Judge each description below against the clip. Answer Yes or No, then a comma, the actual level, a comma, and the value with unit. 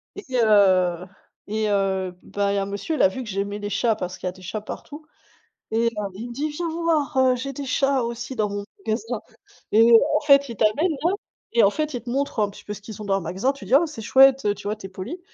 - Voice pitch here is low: No, high, 220 Hz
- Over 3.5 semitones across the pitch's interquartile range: Yes, average, 5.3 semitones